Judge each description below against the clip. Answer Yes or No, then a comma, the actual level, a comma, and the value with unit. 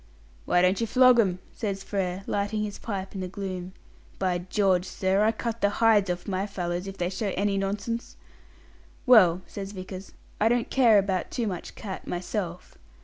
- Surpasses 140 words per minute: Yes, average, 180 wpm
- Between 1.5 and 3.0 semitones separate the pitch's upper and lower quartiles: Yes, narrow, 2.4 semitones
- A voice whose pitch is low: No, high, 195 Hz